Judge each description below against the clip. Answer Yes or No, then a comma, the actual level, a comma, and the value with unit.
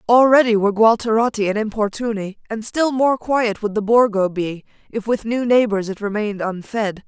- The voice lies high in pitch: Yes, high, 220 Hz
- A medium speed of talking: Yes, average, 170 wpm